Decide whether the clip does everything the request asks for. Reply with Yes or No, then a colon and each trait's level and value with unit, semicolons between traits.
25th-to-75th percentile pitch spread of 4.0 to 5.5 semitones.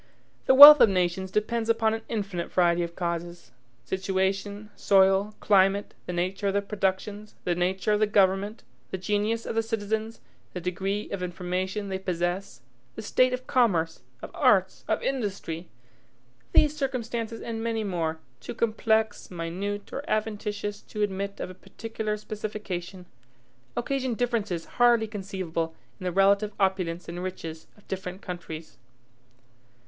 No: average, 3.2 semitones